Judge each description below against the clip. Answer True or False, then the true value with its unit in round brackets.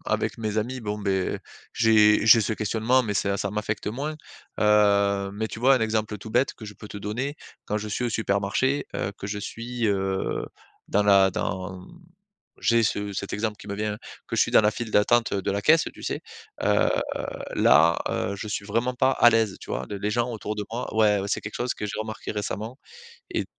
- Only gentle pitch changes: True (2.1 semitones)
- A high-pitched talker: False (105 Hz)